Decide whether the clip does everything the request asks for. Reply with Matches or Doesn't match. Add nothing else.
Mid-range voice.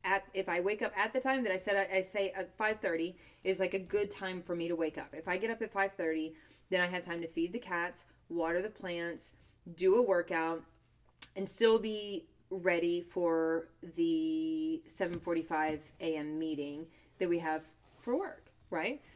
Matches